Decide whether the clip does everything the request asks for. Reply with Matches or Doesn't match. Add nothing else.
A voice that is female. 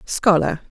Matches